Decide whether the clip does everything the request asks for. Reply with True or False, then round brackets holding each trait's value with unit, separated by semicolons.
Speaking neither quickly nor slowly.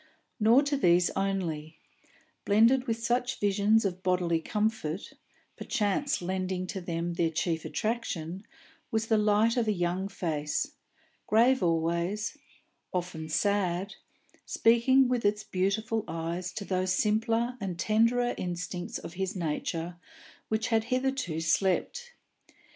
False (125 wpm)